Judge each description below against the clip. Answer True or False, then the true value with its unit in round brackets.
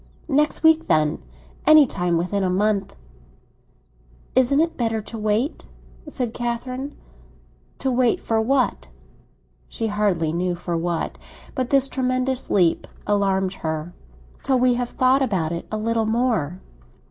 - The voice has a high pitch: True (225 Hz)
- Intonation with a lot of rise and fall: True (5.9 semitones)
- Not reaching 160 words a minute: True (135 wpm)